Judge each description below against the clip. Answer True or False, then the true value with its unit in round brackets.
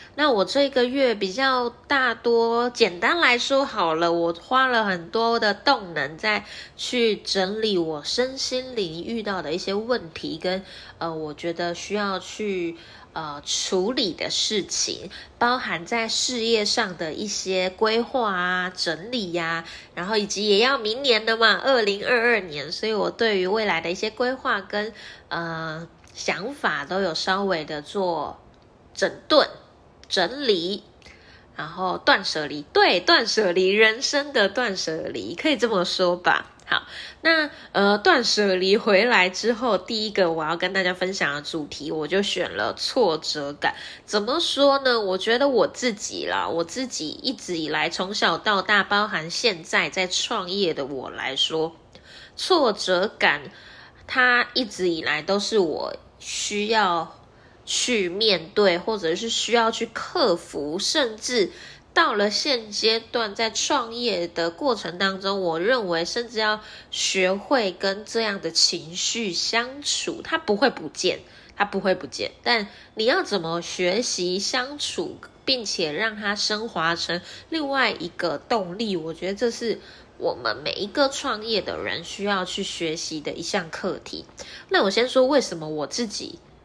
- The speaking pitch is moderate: False (205 Hz)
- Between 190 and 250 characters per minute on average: True (220 characters per minute)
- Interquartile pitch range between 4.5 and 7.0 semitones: True (5.3 semitones)